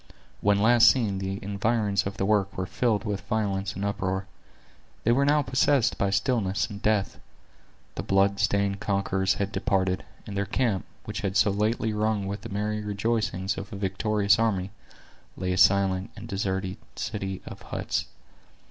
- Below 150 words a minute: No, average, 165 wpm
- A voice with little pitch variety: Yes, narrow, 1.8 semitones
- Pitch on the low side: Yes, low, 100 Hz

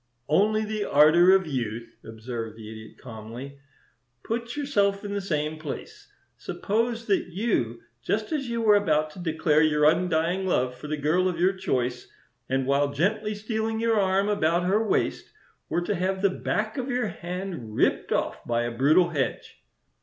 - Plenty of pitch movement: Yes, wide, 6.8 semitones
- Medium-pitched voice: Yes, medium, 175 Hz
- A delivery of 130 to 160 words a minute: No, average, 170 wpm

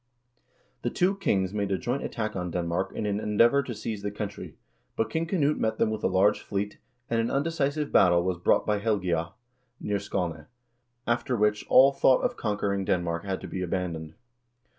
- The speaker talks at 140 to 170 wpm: No, average, 190 wpm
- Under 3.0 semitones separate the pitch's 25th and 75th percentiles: No, average, 4.1 semitones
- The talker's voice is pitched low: Yes, low, 105 Hz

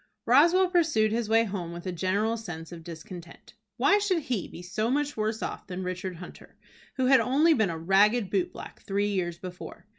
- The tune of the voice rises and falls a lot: Yes, wide, 6.0 semitones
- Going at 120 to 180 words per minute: No, average, 200 wpm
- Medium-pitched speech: No, high, 205 Hz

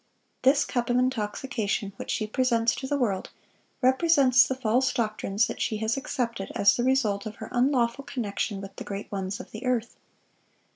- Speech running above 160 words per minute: Yes, average, 180 wpm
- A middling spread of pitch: Yes, average, 3.5 semitones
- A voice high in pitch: Yes, high, 235 Hz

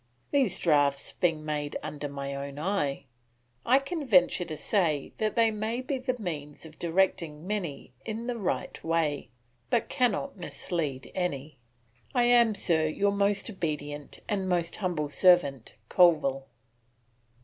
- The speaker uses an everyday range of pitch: No, wide, 6.1 semitones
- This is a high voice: No, medium, 175 Hz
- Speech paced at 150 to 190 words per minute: No, average, 140 wpm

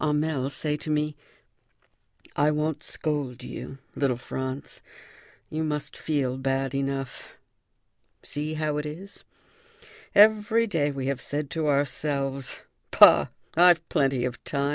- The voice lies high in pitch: No, medium, 145 Hz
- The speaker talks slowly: Yes, slow, 125 wpm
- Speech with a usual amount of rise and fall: No, narrow, 2.3 semitones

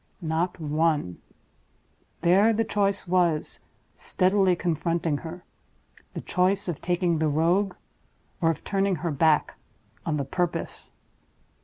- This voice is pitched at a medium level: Yes, medium, 175 Hz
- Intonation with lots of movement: No, average, 2.7 semitones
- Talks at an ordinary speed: No, slow, 120 wpm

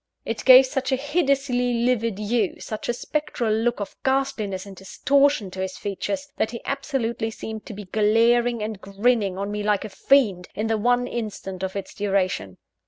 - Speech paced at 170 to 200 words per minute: Yes, average, 180 wpm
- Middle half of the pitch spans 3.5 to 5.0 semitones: Yes, average, 3.8 semitones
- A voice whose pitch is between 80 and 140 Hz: No, high, 225 Hz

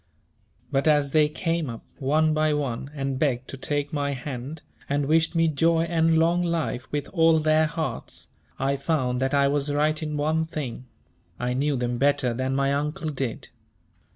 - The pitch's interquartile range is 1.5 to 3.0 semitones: Yes, average, 2.7 semitones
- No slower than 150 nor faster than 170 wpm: No, average, 180 wpm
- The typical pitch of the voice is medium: Yes, medium, 145 Hz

